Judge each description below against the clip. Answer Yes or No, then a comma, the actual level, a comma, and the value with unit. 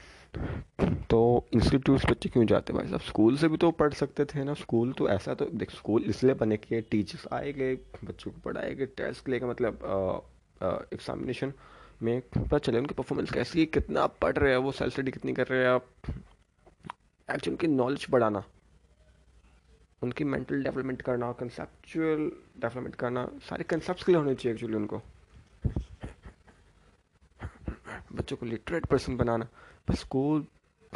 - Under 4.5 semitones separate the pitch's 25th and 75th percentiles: No, average, 4.8 semitones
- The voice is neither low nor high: No, low, 120 Hz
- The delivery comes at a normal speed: Yes, average, 150 wpm